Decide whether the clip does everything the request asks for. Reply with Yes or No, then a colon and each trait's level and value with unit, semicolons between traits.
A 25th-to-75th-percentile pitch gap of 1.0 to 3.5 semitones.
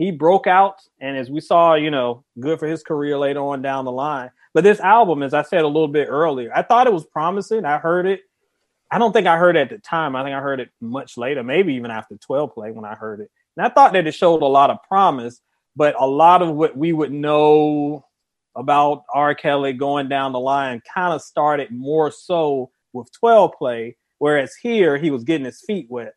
No: average, 3.9 semitones